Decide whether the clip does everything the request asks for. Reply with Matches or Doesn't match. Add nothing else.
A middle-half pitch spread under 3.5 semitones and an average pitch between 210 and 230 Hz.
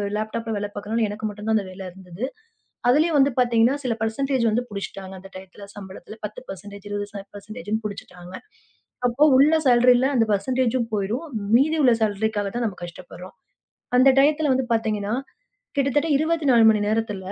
Doesn't match